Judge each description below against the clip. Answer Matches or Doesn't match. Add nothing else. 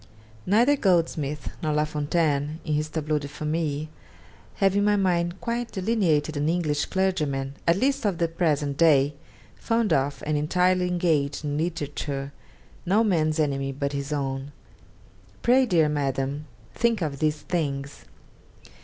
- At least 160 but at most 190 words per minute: Doesn't match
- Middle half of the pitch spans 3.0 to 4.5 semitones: Matches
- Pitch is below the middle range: Doesn't match